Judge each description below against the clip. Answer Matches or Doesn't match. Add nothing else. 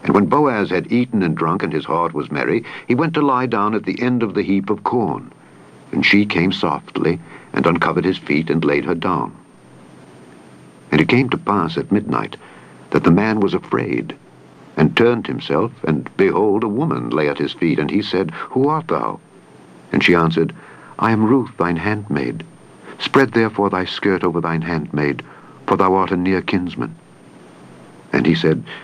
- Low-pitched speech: Matches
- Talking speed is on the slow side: Doesn't match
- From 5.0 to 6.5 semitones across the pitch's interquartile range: Matches